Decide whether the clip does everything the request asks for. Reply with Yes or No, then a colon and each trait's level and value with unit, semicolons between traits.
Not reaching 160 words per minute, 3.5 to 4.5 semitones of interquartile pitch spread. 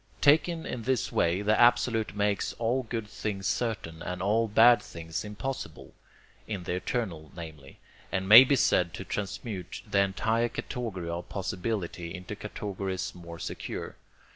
Yes: average, 145 wpm; average, 4.2 semitones